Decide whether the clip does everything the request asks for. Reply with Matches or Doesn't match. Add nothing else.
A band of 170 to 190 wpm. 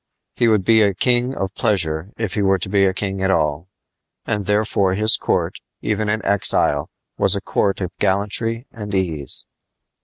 Matches